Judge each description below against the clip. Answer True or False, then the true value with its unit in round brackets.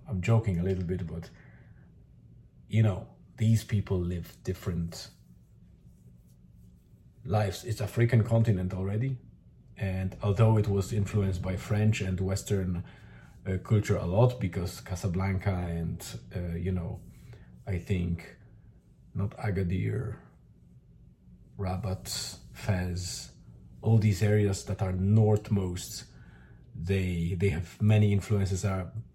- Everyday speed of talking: False (110 wpm)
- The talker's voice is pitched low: True (95 Hz)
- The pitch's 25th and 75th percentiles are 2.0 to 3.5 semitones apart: True (2.9 semitones)